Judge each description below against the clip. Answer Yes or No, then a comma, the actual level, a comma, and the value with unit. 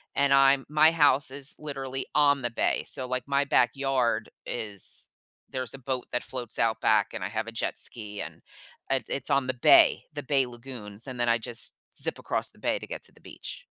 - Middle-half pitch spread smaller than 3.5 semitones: Yes, average, 2.9 semitones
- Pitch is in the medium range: No, low, 130 Hz